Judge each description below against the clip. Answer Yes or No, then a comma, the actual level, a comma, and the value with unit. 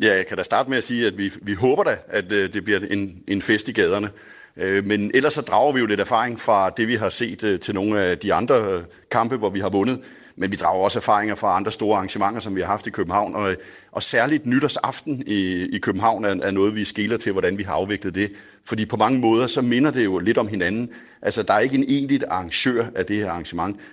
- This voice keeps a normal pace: No, fast, 250 wpm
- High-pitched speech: No, low, 105 Hz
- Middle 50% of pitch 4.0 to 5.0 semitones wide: No, average, 2.8 semitones